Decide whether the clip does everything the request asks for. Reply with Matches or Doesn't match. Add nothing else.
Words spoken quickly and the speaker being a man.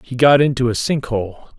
Matches